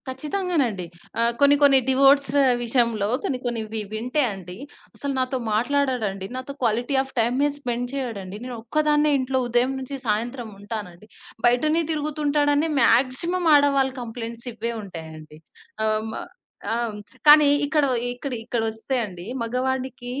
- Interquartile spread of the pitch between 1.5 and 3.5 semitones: No, average, 4.0 semitones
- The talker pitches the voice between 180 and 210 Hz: No, high, 245 Hz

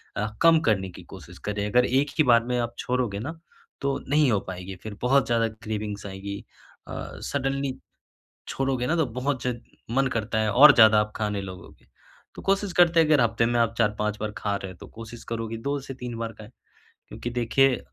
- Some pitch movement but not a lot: Yes, average, 4.2 semitones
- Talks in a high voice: No, low, 115 Hz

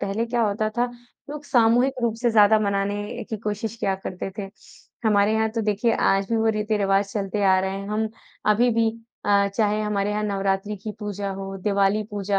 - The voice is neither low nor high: No, high, 210 Hz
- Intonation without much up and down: Yes, narrow, 1.9 semitones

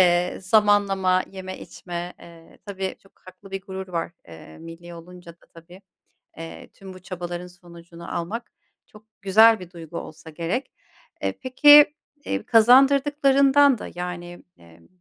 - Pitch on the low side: No, medium, 185 Hz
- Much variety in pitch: No, average, 3.7 semitones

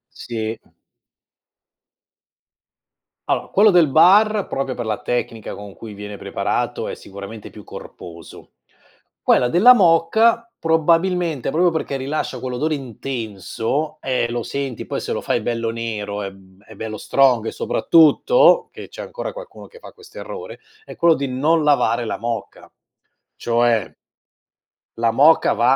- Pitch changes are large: Yes, wide, 6.7 semitones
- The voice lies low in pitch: Yes, low, 130 Hz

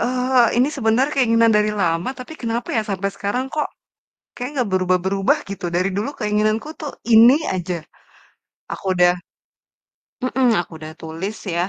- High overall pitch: Yes, high, 215 Hz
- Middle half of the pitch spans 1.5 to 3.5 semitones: No, average, 5.1 semitones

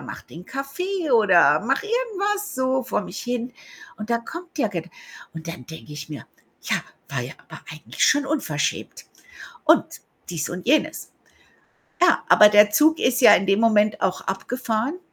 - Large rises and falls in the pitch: Yes, wide, 7.8 semitones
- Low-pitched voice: No, high, 230 Hz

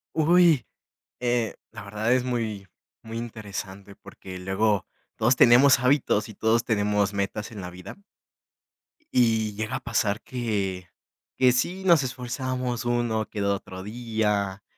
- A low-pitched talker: Yes, low, 110 Hz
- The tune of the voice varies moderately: Yes, average, 3.4 semitones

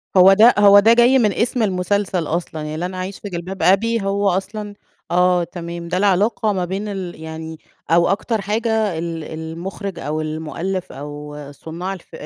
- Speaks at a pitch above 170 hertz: Yes, medium, 185 Hz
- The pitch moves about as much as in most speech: Yes, average, 3.4 semitones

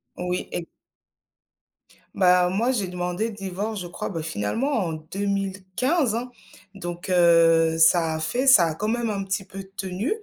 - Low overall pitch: No, medium, 185 Hz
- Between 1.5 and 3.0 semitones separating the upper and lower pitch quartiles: No, average, 3.7 semitones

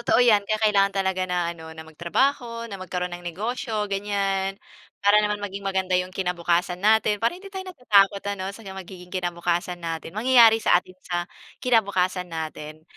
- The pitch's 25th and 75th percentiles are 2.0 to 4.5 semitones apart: Yes, average, 3.1 semitones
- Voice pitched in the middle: No, high, 195 Hz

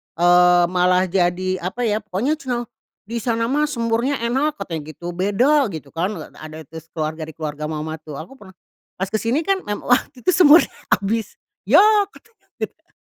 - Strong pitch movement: Yes, wide, 6.6 semitones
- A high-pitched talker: Yes, high, 195 Hz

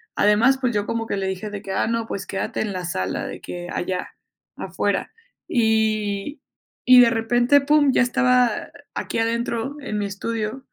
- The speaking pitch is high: Yes, high, 225 Hz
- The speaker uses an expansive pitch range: No, average, 3.5 semitones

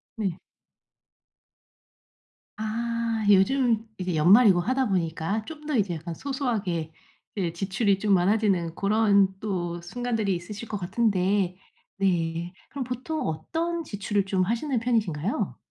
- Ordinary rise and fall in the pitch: Yes, average, 4.4 semitones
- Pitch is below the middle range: No, high, 200 Hz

